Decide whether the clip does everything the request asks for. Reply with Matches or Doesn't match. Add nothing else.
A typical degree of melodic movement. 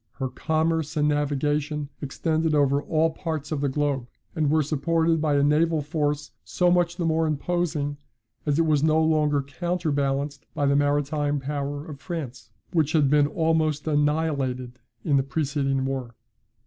Doesn't match